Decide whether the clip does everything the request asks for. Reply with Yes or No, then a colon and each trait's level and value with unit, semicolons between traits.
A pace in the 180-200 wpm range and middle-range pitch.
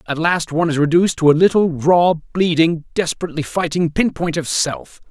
Yes: average, 190 wpm; medium, 165 Hz